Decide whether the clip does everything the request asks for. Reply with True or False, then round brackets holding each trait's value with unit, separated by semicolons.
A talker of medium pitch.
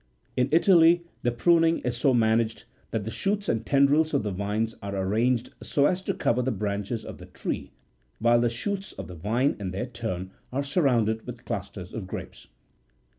False (120 Hz)